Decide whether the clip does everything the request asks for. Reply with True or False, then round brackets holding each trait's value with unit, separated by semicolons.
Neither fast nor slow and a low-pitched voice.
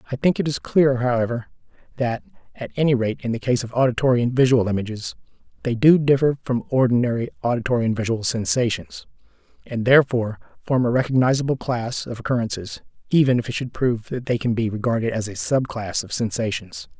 True (180 wpm; 120 Hz)